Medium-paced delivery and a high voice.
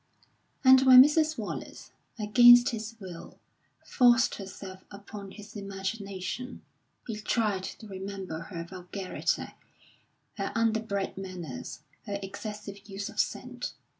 No: slow, 110 wpm; high, 200 Hz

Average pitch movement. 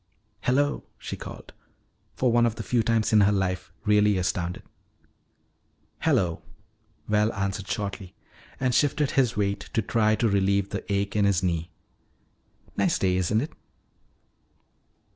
Yes: average, 3.1 semitones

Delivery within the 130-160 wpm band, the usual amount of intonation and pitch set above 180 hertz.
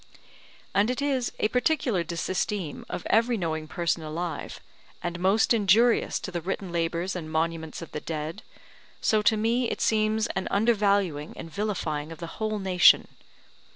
Yes: average, 155 wpm; average, 4.6 semitones; high, 190 Hz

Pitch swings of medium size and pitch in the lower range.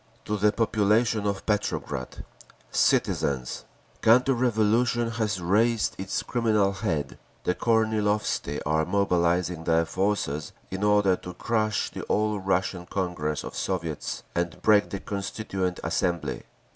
Yes: average, 3.6 semitones; low, 100 Hz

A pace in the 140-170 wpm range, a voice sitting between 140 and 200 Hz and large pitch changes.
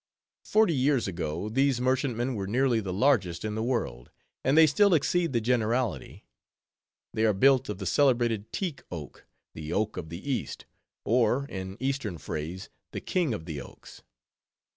No: average, 165 wpm; low, 115 Hz; wide, 6.1 semitones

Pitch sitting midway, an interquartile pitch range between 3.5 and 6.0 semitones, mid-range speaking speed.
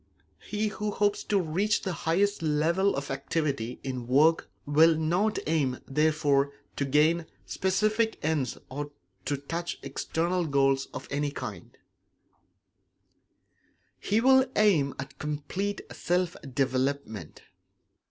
No: medium, 155 Hz; average, 5.2 semitones; slow, 115 wpm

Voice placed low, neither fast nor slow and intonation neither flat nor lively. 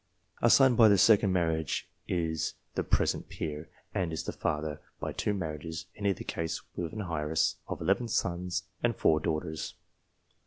Yes: very low, 85 Hz; average, 165 wpm; average, 3.7 semitones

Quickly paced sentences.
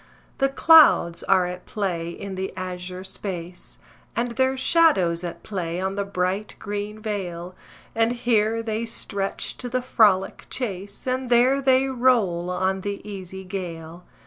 No: average, 145 wpm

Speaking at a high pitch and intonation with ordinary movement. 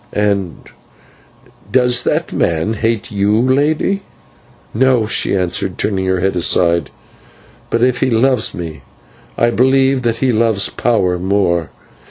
No: low, 110 Hz; average, 5.0 semitones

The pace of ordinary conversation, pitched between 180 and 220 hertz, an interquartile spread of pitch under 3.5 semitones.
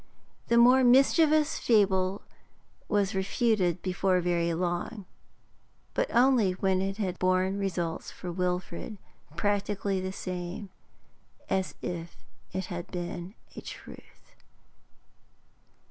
No: slow, 105 wpm; high, 190 Hz; narrow, 2.6 semitones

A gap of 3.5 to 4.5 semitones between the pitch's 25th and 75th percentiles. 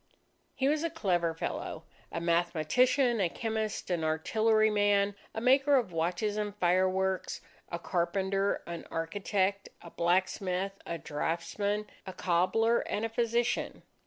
Yes: average, 4.2 semitones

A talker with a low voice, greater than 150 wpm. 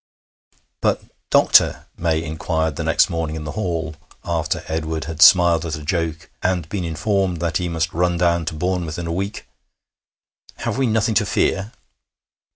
Yes: very low, 85 Hz; average, 165 wpm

